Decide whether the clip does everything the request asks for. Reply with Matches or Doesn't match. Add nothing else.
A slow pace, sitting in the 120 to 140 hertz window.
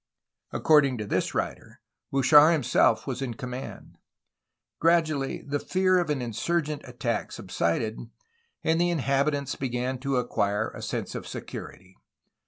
Matches